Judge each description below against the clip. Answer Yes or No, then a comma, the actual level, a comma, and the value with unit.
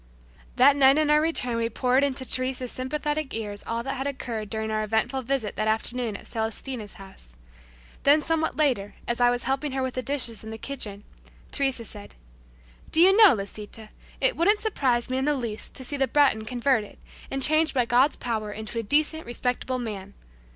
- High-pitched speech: Yes, very high, 250 Hz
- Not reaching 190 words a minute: No, average, 195 wpm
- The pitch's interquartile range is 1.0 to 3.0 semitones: No, average, 4.1 semitones